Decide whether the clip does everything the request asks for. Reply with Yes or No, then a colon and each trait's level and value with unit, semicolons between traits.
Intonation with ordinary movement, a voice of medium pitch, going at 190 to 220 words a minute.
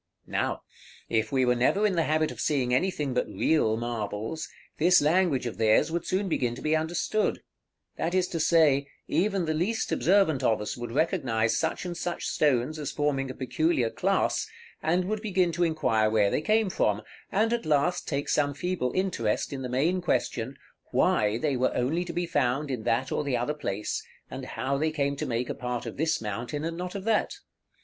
No: wide, 5.9 semitones; medium, 150 Hz; average, 200 wpm